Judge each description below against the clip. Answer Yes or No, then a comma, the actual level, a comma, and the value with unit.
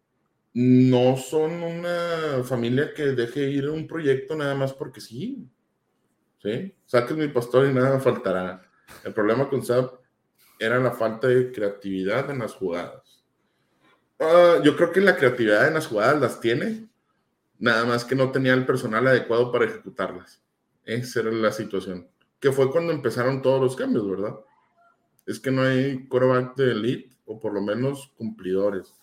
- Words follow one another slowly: No, average, 160 wpm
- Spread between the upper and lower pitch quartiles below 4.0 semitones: Yes, average, 3.3 semitones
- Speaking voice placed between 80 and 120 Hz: No, low, 130 Hz